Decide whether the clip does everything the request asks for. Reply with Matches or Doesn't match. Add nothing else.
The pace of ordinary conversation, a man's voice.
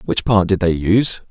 Doesn't match